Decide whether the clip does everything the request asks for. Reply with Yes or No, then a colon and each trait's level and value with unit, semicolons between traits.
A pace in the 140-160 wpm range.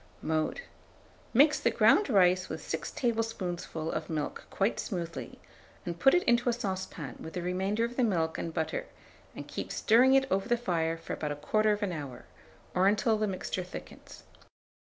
No: average, 175 wpm